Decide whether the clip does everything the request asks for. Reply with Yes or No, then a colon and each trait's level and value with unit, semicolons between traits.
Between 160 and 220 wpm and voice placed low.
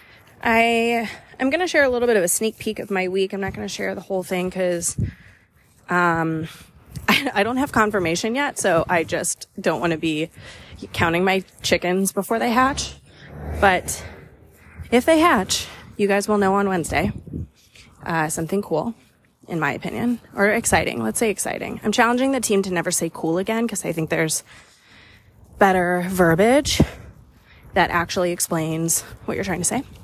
No: average, 175 wpm; medium, 185 Hz